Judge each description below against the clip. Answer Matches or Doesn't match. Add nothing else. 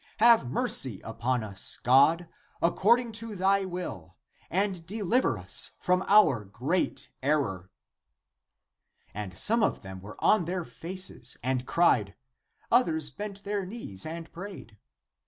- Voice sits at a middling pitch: Matches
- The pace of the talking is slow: Matches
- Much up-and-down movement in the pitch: Matches